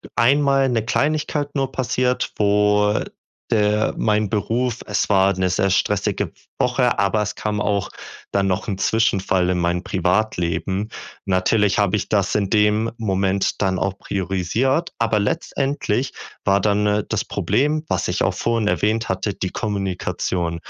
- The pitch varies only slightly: No, average, 3.0 semitones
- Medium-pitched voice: No, low, 105 Hz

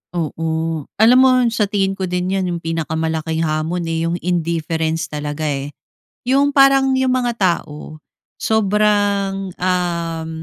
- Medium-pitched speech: Yes, medium, 175 Hz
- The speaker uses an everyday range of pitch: Yes, average, 4.1 semitones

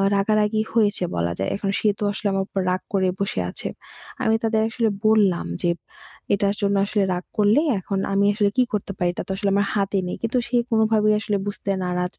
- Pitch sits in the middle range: No, high, 205 Hz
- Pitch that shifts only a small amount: Yes, narrow, 1.9 semitones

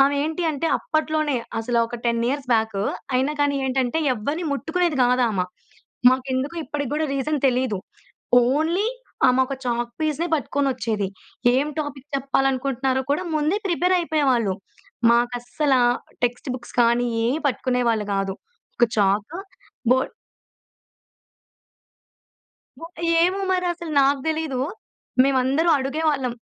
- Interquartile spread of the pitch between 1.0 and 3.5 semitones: No, average, 4.0 semitones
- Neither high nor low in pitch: No, very high, 270 Hz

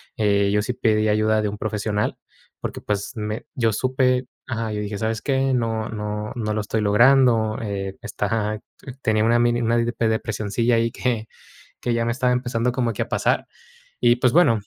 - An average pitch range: No, narrow, 2.1 semitones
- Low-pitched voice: Yes, low, 110 Hz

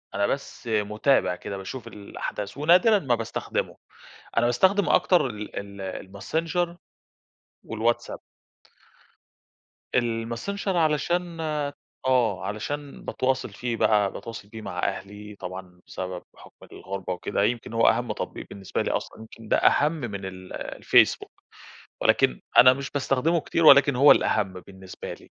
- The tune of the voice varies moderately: No, wide, 6.1 semitones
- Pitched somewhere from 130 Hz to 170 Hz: No, low, 115 Hz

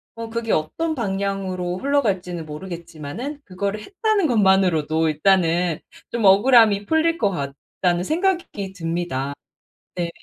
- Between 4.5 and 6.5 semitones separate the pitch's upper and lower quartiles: Yes, average, 5.3 semitones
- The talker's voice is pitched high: Yes, high, 195 Hz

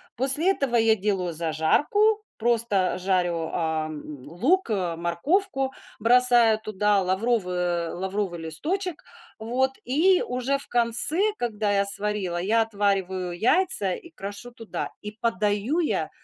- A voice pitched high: Yes, high, 210 Hz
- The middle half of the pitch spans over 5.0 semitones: Yes, wide, 5.5 semitones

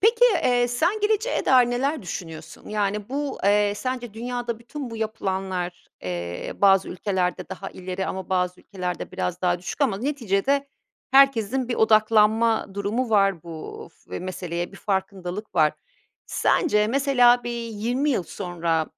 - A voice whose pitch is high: Yes, high, 210 Hz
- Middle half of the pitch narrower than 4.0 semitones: No, average, 5.0 semitones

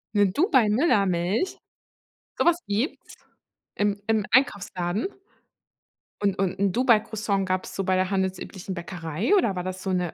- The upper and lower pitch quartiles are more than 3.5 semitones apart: No, average, 2.9 semitones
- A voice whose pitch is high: Yes, high, 195 Hz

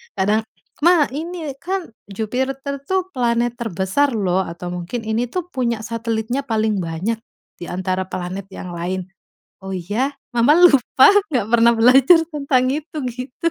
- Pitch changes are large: Yes, wide, 6.2 semitones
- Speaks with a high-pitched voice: Yes, high, 235 Hz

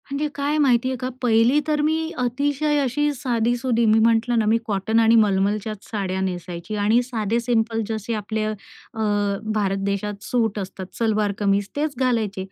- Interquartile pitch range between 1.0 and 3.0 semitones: No, average, 3.5 semitones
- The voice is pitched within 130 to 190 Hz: No, high, 225 Hz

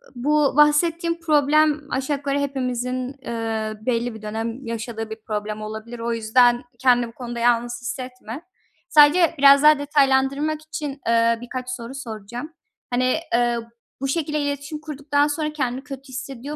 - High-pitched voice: Yes, very high, 260 Hz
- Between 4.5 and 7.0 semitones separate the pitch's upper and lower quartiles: No, average, 3.8 semitones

